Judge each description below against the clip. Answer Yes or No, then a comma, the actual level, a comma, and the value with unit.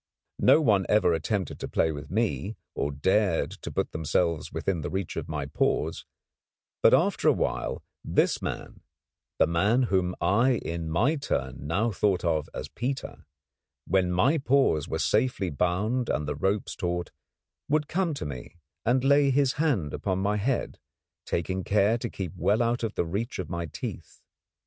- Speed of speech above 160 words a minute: Yes, average, 170 wpm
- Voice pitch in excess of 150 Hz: No, very low, 95 Hz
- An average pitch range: No, wide, 6.0 semitones